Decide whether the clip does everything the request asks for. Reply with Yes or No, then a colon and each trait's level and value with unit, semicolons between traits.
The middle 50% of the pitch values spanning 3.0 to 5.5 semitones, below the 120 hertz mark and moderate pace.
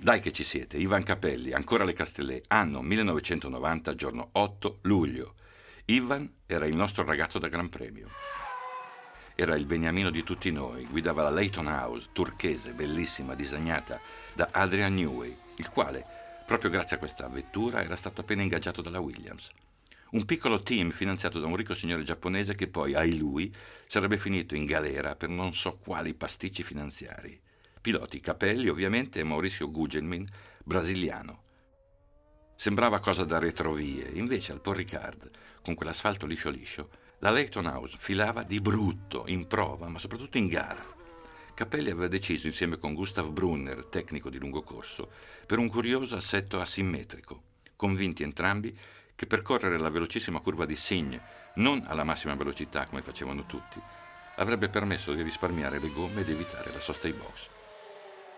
Yes: average, 4.4 semitones; very low, 90 Hz; average, 150 wpm